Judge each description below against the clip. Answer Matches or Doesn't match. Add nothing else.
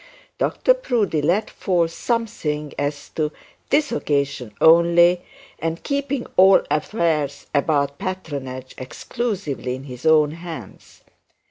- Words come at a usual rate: Doesn't match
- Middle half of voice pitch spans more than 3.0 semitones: Matches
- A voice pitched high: Doesn't match